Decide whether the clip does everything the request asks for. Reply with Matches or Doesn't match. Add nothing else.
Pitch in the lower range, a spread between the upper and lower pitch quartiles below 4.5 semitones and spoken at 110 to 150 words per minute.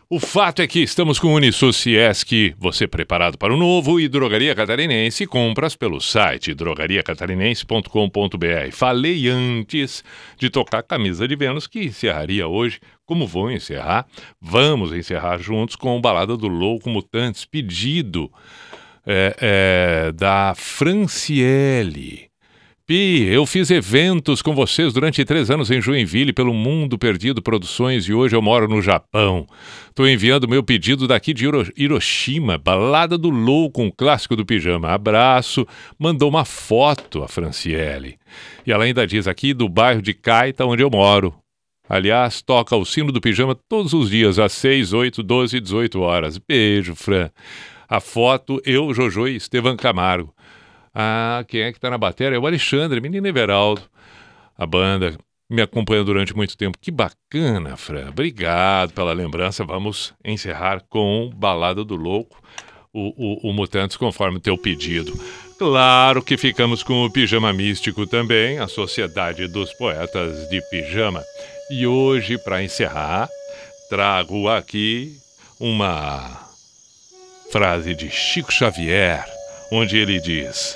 Doesn't match